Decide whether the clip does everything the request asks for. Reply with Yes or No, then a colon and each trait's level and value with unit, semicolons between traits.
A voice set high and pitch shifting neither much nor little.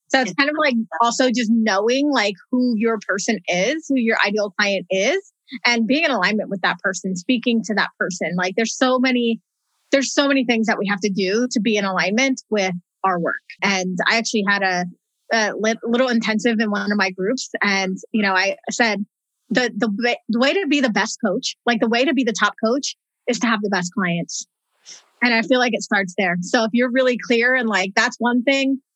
Yes: high, 225 Hz; average, 3.8 semitones